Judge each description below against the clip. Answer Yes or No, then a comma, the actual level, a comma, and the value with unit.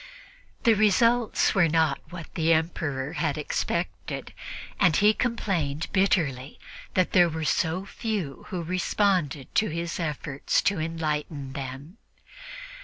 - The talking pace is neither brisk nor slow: No, slow, 120 wpm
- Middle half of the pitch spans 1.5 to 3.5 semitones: No, average, 4.3 semitones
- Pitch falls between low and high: Yes, medium, 165 Hz